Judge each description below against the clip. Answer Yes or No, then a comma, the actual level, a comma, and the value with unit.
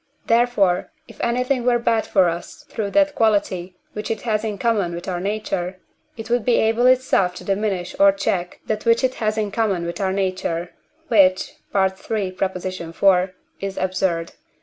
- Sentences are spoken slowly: No, average, 170 wpm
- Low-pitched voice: No, high, 195 Hz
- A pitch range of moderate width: Yes, average, 3.5 semitones